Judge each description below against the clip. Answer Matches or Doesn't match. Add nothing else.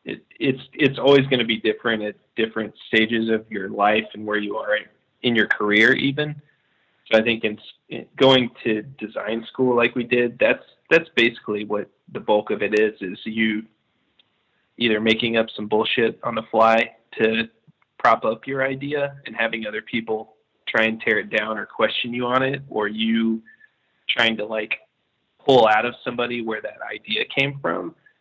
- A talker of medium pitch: Doesn't match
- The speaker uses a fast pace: Doesn't match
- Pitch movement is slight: Matches